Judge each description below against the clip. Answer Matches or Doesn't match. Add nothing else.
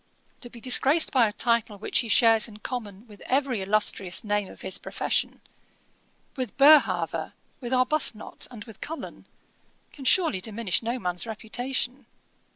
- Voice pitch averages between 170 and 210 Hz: Doesn't match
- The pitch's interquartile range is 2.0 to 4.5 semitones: Matches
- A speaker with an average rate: Matches